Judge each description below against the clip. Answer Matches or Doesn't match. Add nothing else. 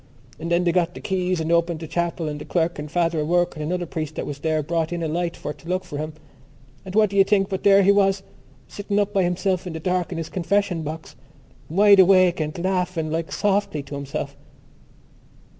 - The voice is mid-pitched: Matches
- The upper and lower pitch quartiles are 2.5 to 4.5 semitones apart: Matches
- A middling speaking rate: Doesn't match